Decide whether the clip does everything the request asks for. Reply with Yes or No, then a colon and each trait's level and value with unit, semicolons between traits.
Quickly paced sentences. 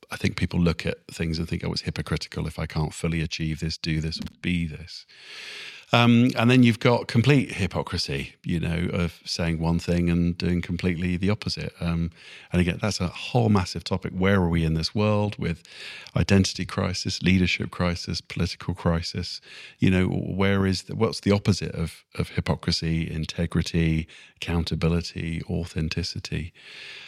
No: average, 170 wpm